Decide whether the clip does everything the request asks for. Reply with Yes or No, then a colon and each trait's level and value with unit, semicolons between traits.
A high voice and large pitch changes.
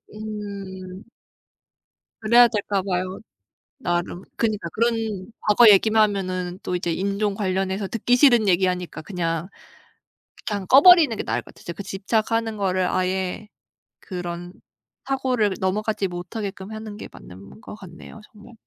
No: high, 200 Hz; average, 2.9 semitones